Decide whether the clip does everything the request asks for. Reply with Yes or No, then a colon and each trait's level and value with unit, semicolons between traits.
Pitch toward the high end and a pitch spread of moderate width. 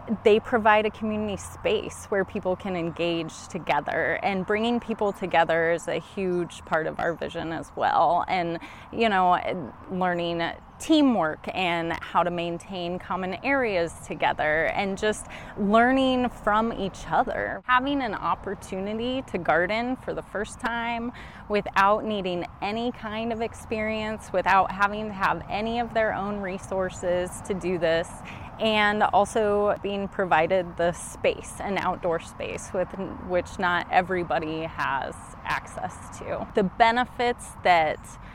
Yes: high, 195 Hz; average, 3.9 semitones